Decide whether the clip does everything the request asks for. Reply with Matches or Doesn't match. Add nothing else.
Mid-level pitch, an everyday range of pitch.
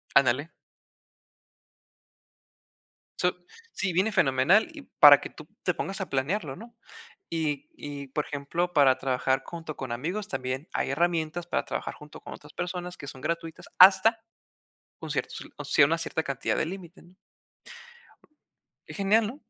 Matches